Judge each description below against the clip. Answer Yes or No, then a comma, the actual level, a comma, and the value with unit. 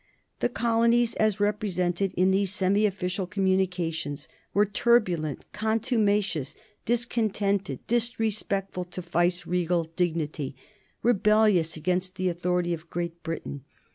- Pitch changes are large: No, average, 3.5 semitones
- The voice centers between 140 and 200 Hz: Yes, medium, 185 Hz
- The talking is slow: Yes, slow, 105 wpm